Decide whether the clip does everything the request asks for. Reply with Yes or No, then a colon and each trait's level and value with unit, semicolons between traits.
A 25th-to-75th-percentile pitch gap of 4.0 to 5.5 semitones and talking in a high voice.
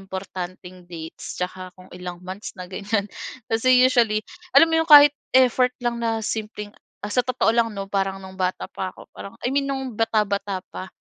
Yes: average, 4.3 semitones; high, 205 Hz